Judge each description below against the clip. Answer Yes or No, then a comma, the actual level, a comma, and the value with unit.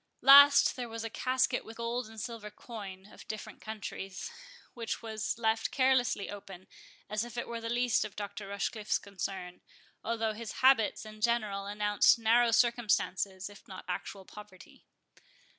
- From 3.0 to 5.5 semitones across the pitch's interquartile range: No, narrow, 2.6 semitones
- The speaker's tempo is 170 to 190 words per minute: No, average, 155 wpm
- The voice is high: Yes, high, 220 Hz